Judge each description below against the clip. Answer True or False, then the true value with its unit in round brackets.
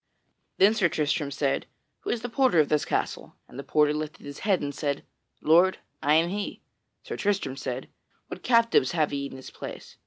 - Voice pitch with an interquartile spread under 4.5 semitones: False (5.4 semitones)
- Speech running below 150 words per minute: False (195 wpm)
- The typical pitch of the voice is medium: True (155 Hz)